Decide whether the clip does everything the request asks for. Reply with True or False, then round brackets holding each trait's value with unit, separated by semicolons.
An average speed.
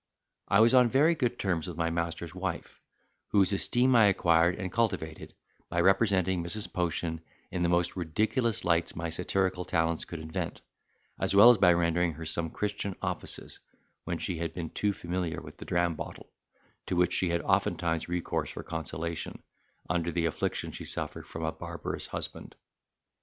True (170 wpm)